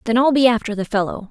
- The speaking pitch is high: Yes, high, 230 Hz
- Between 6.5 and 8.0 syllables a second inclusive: Yes, 6.8 syllables/s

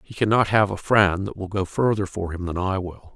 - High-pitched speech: No, very low, 95 Hz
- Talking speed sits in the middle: No, fast, 265 wpm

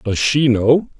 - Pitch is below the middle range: Yes, low, 125 Hz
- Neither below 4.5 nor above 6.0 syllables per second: No, 3.8 syllables/s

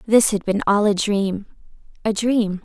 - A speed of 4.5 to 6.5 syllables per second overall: No, 4.2 syllables/s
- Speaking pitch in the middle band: No, high, 205 Hz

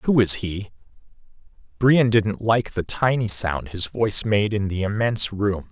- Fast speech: No, average, 170 wpm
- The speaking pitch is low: Yes, low, 105 Hz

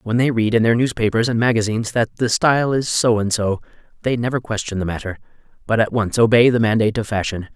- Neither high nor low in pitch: No, low, 115 Hz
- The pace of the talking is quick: Yes, fast, 220 wpm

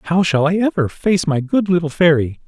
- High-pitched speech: No, medium, 170 Hz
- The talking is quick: Yes, fast, 220 wpm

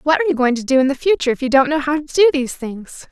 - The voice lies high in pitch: Yes, very high, 280 Hz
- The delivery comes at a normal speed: No, fast, 345 wpm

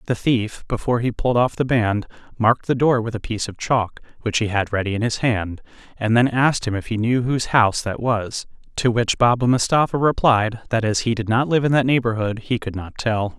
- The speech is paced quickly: Yes, fast, 235 wpm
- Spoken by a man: Yes, male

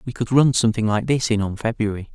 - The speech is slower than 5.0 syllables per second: No, 6.4 syllables/s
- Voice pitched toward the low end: Yes, low, 115 Hz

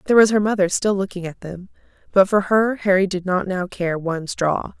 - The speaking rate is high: Yes, fast, 225 wpm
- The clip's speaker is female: Yes, female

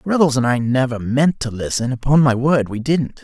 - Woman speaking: No, male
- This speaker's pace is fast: Yes, fast, 220 wpm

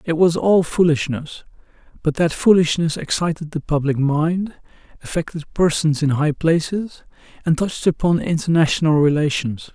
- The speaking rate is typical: No, slow, 130 wpm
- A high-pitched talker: No, medium, 160 Hz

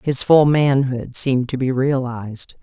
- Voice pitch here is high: No, low, 130 Hz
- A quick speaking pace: No, average, 160 wpm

